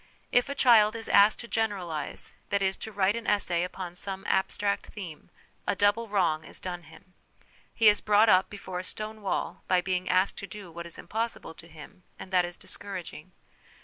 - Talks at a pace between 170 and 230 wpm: Yes, average, 195 wpm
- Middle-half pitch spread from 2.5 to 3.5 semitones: Yes, average, 2.9 semitones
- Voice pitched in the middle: No, high, 195 Hz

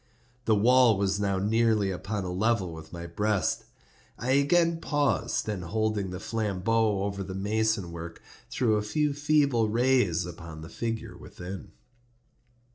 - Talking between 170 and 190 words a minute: No, average, 145 wpm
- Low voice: Yes, low, 105 Hz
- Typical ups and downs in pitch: Yes, average, 3.8 semitones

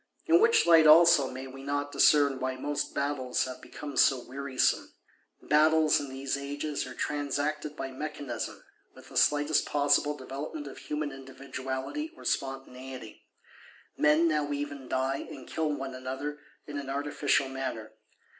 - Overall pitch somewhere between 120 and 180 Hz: Yes, medium, 140 Hz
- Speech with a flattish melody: Yes, narrow, 2.0 semitones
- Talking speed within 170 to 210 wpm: No, average, 145 wpm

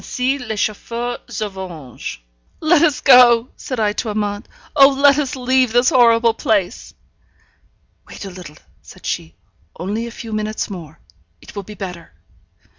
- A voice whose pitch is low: No, high, 225 Hz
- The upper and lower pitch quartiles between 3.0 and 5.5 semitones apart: Yes, average, 4.1 semitones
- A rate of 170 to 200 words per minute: No, average, 155 wpm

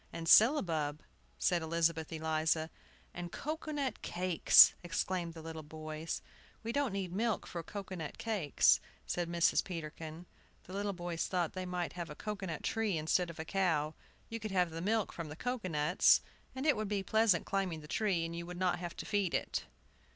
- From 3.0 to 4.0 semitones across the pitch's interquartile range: Yes, average, 3.5 semitones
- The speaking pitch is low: No, medium, 175 Hz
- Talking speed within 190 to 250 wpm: Yes, average, 195 wpm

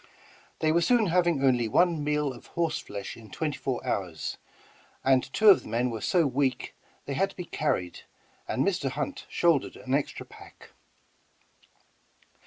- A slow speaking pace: No, average, 165 wpm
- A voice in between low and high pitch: Yes, medium, 145 Hz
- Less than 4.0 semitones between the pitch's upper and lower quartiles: No, wide, 5.5 semitones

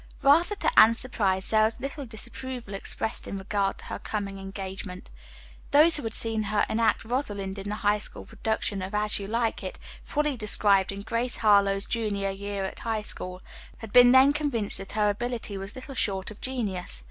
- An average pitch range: Yes, average, 3.3 semitones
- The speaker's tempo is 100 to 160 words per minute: No, average, 190 wpm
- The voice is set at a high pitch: Yes, high, 215 Hz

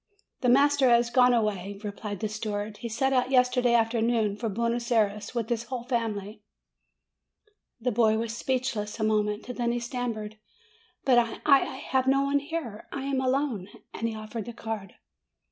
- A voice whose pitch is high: Yes, high, 235 Hz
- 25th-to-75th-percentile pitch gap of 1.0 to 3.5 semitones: Yes, average, 2.7 semitones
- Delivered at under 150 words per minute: No, average, 180 wpm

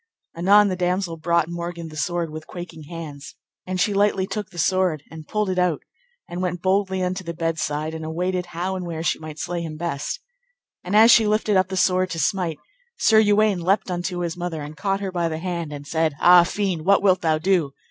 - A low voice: No, medium, 175 Hz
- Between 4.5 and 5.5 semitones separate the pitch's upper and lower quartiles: No, narrow, 2.6 semitones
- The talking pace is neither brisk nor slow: No, fast, 220 wpm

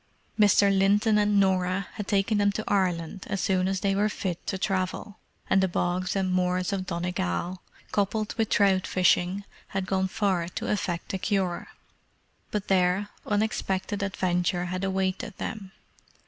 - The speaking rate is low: No, average, 155 wpm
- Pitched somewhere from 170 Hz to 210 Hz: Yes, high, 190 Hz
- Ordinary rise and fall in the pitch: No, narrow, 1.8 semitones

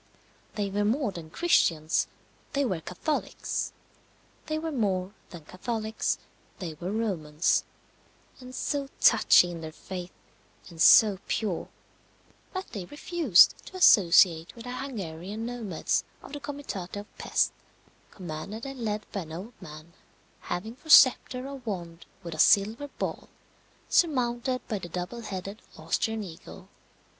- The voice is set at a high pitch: Yes, high, 205 Hz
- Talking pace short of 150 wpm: Yes, slow, 135 wpm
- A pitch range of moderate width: No, wide, 6.2 semitones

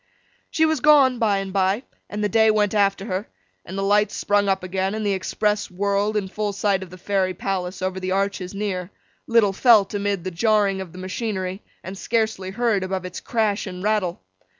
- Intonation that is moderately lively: No, narrow, 2.0 semitones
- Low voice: No, high, 200 Hz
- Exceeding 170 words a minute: Yes, average, 200 wpm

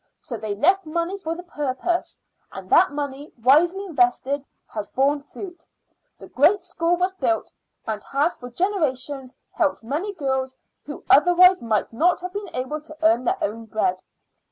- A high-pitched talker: Yes, very high, 300 Hz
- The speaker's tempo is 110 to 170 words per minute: Yes, average, 160 wpm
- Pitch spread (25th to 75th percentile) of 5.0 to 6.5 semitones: Yes, wide, 5.4 semitones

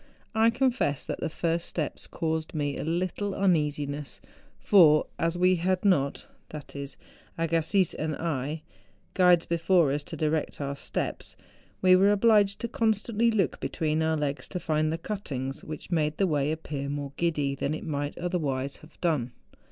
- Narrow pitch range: No, average, 4.0 semitones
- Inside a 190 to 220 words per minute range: No, average, 160 wpm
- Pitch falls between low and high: Yes, medium, 160 Hz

